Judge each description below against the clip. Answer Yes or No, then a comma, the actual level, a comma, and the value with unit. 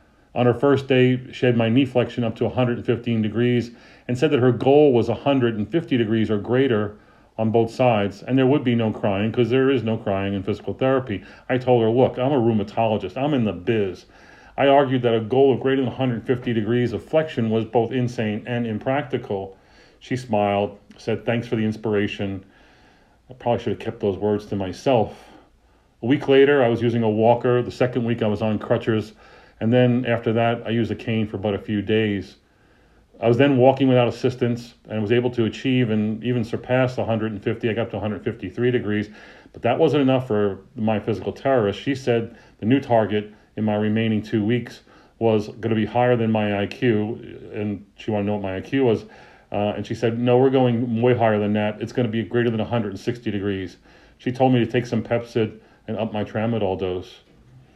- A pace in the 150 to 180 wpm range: No, fast, 205 wpm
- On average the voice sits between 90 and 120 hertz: Yes, low, 115 Hz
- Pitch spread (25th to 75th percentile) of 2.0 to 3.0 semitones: Yes, average, 2.7 semitones